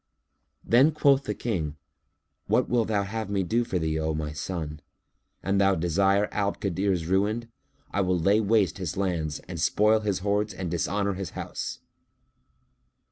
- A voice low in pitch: Yes, low, 100 Hz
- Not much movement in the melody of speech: No, average, 3.4 semitones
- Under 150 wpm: No, average, 165 wpm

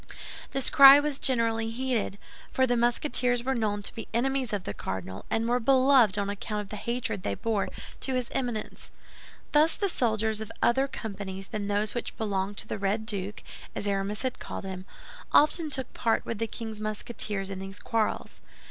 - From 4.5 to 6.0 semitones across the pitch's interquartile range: No, average, 3.7 semitones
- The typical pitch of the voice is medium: No, high, 225 Hz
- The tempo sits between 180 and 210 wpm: Yes, average, 185 wpm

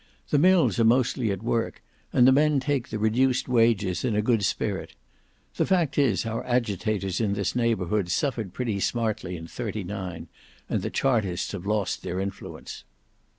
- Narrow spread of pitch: No, average, 4.2 semitones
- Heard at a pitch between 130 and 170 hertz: No, low, 110 Hz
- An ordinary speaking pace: Yes, average, 165 wpm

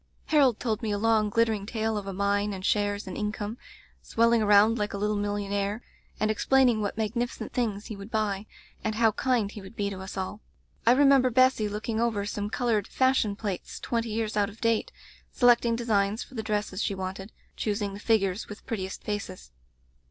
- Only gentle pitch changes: Yes, narrow, 2.2 semitones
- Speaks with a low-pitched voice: No, high, 215 Hz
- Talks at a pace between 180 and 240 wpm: Yes, average, 195 wpm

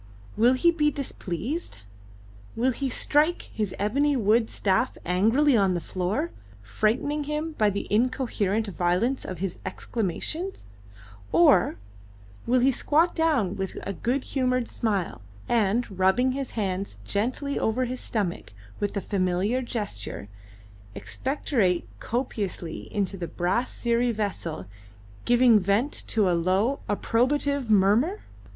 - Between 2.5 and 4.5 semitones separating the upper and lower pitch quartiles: No, average, 5.2 semitones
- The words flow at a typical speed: No, slow, 125 wpm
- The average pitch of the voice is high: Yes, high, 225 Hz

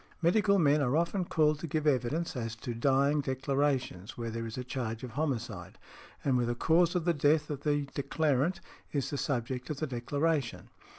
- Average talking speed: Yes, average, 190 wpm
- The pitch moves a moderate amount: Yes, average, 3.9 semitones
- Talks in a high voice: No, medium, 140 Hz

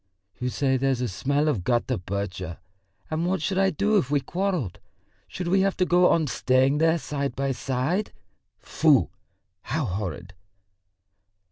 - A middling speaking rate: Yes, average, 155 wpm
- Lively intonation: Yes, wide, 6.1 semitones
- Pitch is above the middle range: No, medium, 140 Hz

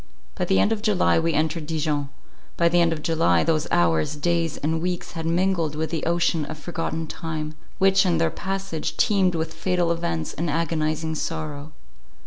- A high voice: No, medium, 165 Hz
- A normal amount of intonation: No, narrow, 2.0 semitones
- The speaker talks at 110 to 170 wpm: No, average, 180 wpm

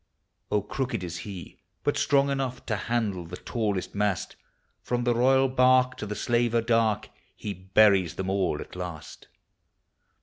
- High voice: No, low, 110 Hz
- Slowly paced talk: No, average, 155 wpm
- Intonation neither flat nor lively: Yes, average, 4.5 semitones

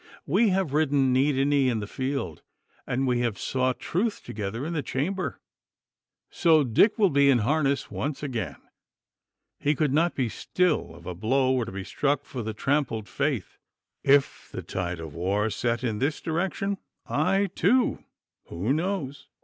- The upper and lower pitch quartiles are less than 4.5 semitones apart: No, average, 5.1 semitones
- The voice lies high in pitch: No, low, 135 Hz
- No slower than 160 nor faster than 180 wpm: Yes, average, 170 wpm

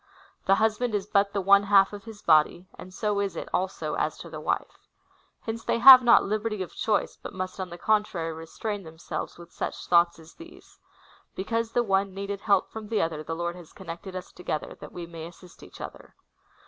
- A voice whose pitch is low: No, high, 195 Hz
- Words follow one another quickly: Yes, fast, 215 wpm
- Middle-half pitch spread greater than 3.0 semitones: Yes, average, 3.7 semitones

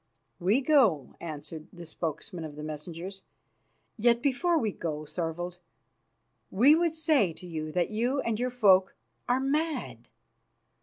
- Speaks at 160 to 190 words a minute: No, average, 140 wpm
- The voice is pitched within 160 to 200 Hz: Yes, high, 190 Hz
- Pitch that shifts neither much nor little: No, wide, 7.8 semitones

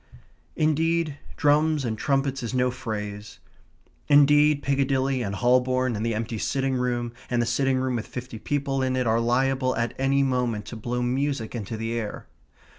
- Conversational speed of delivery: Yes, average, 170 wpm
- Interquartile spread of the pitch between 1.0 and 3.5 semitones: Yes, average, 2.8 semitones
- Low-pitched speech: Yes, low, 130 Hz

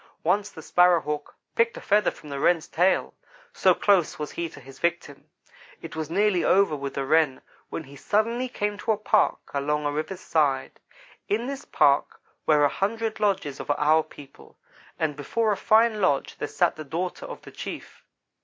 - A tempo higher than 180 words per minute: Yes, average, 190 wpm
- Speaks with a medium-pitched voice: Yes, medium, 165 Hz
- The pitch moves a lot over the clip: Yes, wide, 6.0 semitones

